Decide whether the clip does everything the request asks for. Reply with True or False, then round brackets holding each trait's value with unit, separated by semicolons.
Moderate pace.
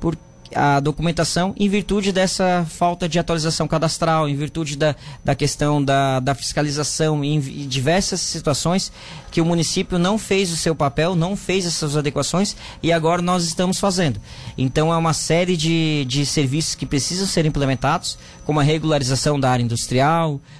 True (155 wpm)